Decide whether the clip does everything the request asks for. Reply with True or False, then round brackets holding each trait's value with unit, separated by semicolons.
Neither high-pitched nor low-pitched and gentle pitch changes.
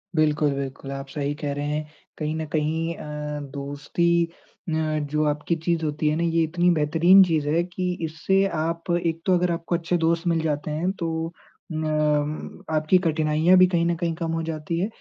True (160 Hz; 2.1 semitones)